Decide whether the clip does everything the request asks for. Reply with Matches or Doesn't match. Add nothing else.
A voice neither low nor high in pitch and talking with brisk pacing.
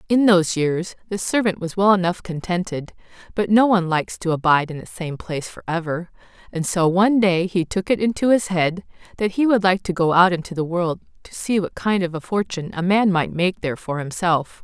Matches